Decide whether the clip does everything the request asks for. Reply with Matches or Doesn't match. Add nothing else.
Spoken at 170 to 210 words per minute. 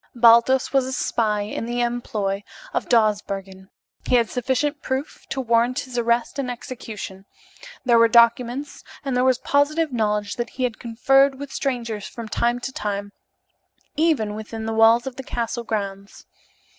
Doesn't match